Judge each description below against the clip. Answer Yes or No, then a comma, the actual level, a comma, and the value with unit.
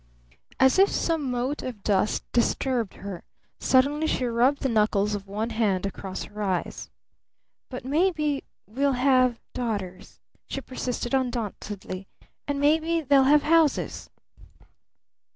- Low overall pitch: No, very high, 250 Hz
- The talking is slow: Yes, slow, 125 wpm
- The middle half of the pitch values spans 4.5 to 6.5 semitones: Yes, average, 5.1 semitones